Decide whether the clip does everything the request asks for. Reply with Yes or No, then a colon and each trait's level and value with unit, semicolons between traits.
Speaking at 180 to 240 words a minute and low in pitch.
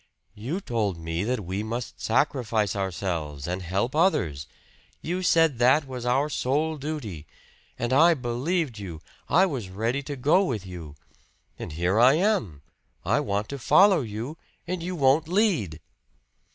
No: average, 150 wpm; low, 120 Hz